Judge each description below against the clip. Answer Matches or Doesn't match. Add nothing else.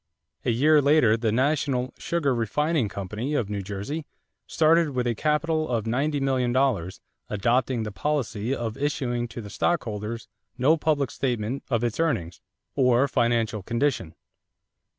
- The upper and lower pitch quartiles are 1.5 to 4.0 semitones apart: Doesn't match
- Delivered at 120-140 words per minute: Matches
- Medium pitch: Doesn't match